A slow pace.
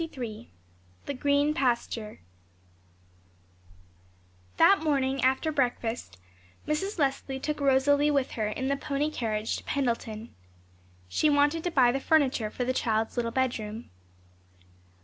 Yes: slow, 130 wpm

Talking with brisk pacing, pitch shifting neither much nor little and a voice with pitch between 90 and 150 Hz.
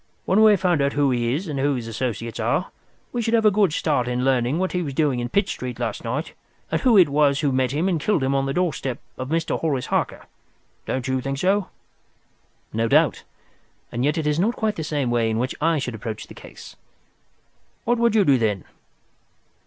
No: fast, 220 wpm; wide, 6.0 semitones; medium, 140 Hz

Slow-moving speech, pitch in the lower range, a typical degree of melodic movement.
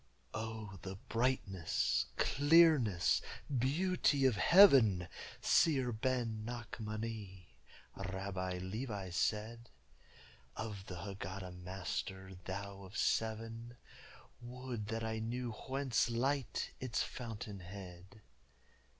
Yes: slow, 90 wpm; low, 110 Hz; average, 4.3 semitones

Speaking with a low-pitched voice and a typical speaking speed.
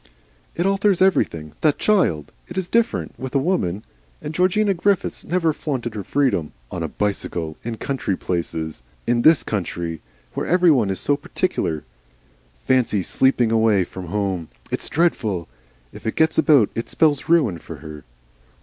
Yes: low, 120 Hz; average, 160 wpm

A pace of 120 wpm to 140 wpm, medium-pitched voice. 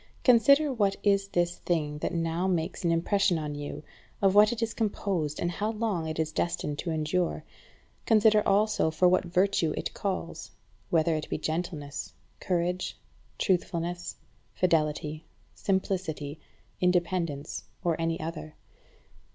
Yes: slow, 135 wpm; medium, 175 Hz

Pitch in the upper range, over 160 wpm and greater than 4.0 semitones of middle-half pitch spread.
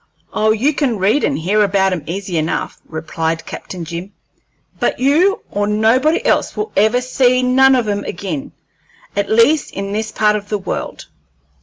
Yes: high, 210 Hz; average, 170 wpm; average, 4.8 semitones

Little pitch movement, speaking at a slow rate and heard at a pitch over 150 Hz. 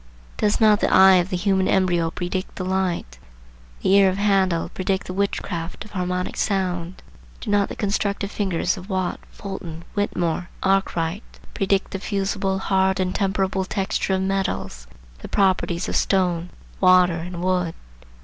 No: narrow, 1.5 semitones; average, 155 wpm; high, 190 Hz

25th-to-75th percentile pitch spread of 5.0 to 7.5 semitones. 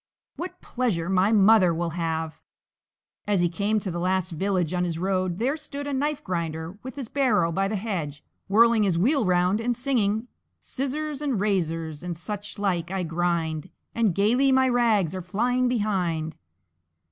Yes: wide, 5.6 semitones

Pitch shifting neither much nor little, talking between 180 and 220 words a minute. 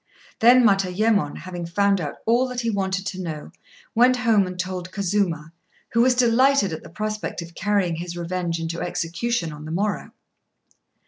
No: average, 4.6 semitones; average, 170 wpm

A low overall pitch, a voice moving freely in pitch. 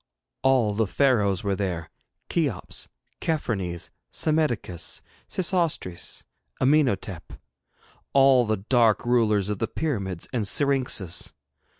Yes: low, 115 Hz; wide, 6.0 semitones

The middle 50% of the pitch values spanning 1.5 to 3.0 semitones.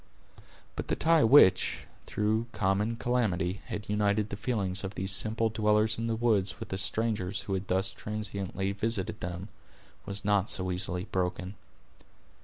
Yes: narrow, 2.6 semitones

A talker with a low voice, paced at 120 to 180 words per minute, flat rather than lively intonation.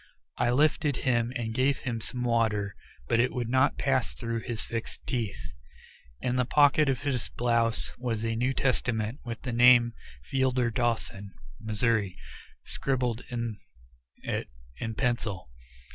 Yes: low, 120 Hz; average, 145 wpm; narrow, 2.1 semitones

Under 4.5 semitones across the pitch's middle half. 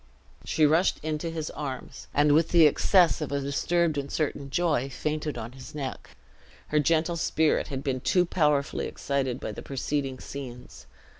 Yes: narrow, 2.6 semitones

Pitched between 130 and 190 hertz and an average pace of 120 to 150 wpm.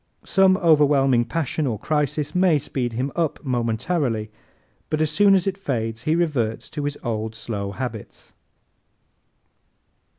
Yes: medium, 140 Hz; slow, 135 wpm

